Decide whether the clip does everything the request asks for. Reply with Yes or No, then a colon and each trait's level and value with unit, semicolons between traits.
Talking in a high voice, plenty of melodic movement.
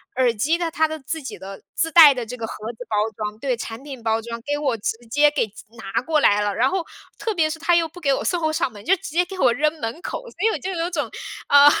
Yes: very high, 285 Hz; wide, 6.1 semitones